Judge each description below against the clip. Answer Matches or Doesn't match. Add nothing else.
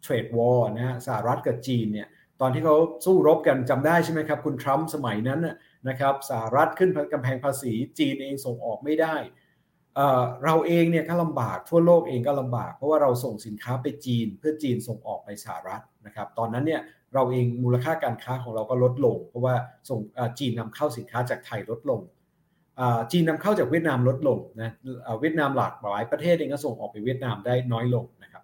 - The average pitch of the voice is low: Matches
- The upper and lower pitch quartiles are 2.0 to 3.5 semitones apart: Doesn't match